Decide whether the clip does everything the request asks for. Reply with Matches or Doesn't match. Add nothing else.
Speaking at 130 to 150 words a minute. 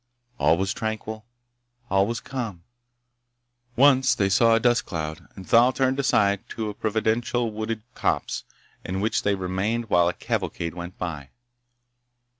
Matches